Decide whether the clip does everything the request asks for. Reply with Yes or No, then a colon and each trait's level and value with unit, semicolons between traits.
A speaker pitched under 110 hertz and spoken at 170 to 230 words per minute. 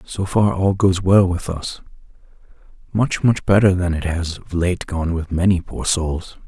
Yes: very low, 90 Hz; average, 175 wpm